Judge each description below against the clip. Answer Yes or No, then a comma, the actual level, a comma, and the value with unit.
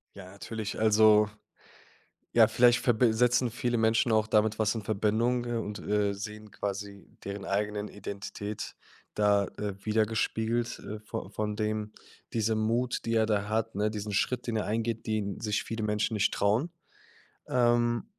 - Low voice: Yes, low, 110 Hz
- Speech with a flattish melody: Yes, narrow, 1.6 semitones